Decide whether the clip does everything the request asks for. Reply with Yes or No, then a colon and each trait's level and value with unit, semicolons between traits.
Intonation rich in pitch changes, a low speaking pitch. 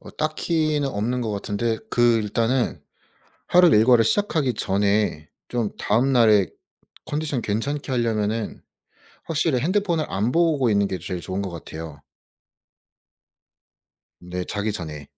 Yes: wide, 6.0 semitones; low, 115 Hz